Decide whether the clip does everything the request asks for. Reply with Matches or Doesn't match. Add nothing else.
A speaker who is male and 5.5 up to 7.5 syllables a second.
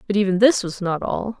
Doesn't match